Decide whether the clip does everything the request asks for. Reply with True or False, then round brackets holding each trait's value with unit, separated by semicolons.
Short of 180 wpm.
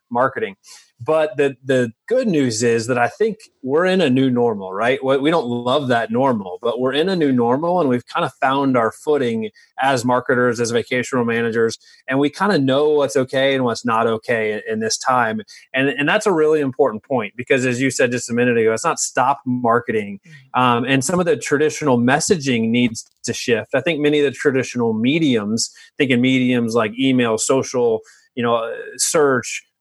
False (195 wpm)